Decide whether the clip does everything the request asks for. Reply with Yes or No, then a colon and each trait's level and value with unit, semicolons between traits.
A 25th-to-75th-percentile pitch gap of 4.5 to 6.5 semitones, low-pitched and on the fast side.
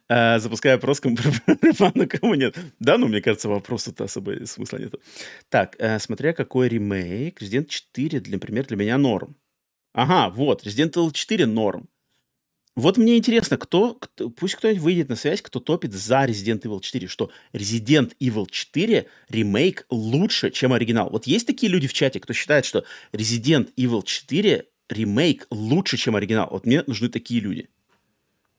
Yes: average, 4.8 semitones; low, 125 Hz; fast, 165 wpm